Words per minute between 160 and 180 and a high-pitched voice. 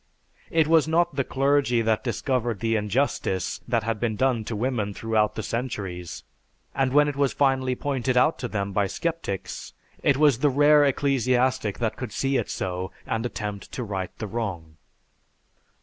No: average, 170 wpm; low, 120 Hz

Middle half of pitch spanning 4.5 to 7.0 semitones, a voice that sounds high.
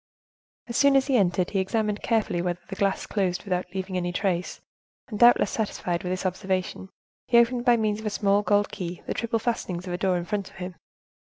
No: average, 3.4 semitones; high, 195 Hz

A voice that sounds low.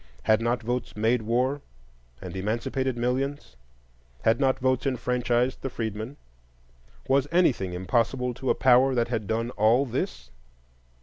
Yes: low, 120 Hz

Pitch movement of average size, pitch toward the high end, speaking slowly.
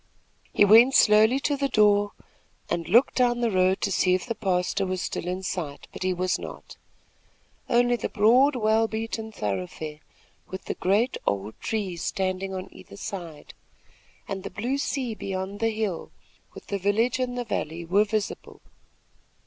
No: average, 3.7 semitones; high, 205 Hz; average, 165 wpm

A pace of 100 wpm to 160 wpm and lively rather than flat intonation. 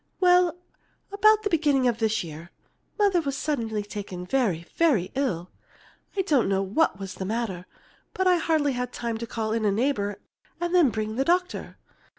No: average, 175 wpm; wide, 8.2 semitones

